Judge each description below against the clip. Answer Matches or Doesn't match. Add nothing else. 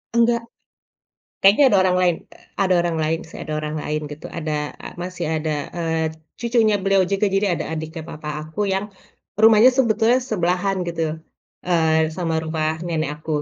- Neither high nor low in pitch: Matches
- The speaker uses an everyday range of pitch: Matches